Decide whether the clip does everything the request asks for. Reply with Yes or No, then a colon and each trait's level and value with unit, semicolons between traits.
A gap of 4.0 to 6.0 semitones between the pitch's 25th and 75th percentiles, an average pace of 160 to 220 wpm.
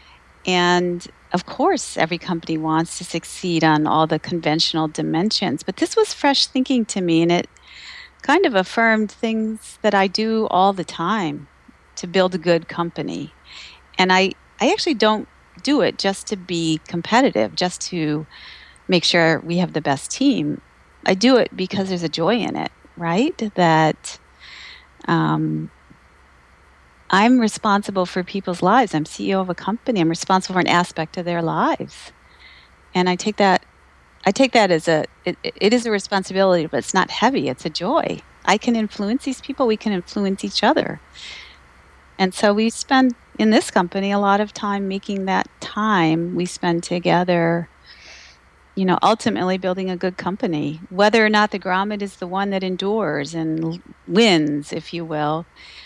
Yes: average, 4.5 semitones; average, 170 wpm